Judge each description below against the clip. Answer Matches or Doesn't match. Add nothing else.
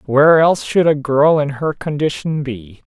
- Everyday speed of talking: Matches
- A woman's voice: Doesn't match